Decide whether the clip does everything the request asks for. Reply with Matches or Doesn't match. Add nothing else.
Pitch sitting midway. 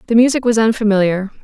Doesn't match